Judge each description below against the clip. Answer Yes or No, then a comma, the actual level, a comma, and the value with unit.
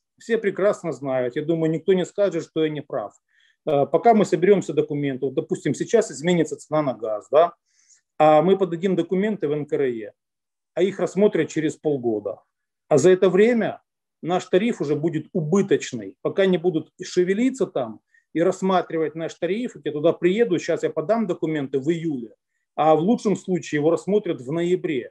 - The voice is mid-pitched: Yes, medium, 170 Hz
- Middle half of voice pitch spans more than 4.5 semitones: No, average, 4.0 semitones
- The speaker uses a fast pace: Yes, fast, 165 wpm